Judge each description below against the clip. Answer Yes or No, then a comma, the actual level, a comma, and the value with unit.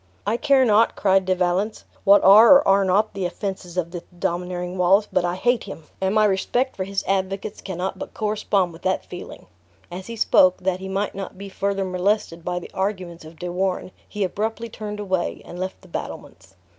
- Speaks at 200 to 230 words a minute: Yes, fast, 205 wpm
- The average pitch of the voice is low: No, high, 190 Hz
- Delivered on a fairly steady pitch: Yes, narrow, 2.3 semitones